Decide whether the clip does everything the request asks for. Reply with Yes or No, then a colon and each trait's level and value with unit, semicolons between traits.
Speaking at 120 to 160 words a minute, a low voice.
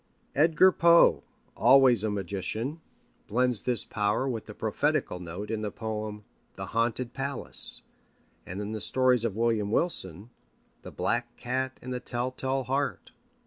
Yes: average, 145 wpm; low, 120 Hz